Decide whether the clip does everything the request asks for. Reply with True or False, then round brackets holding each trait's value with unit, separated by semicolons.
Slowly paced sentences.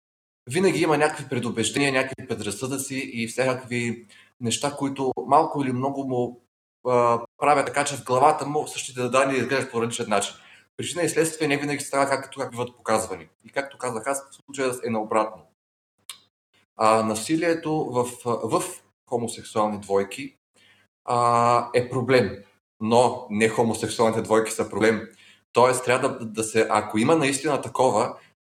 False (145 wpm)